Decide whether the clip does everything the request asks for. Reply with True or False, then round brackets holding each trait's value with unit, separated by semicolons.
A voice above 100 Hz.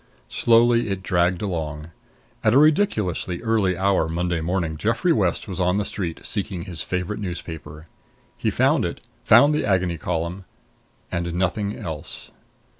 False (90 Hz)